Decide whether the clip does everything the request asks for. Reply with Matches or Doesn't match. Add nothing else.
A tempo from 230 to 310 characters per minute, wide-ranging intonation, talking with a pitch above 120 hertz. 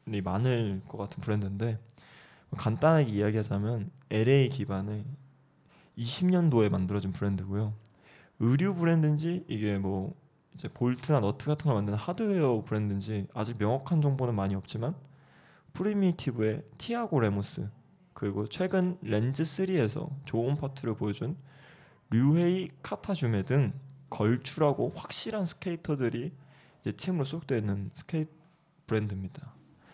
Matches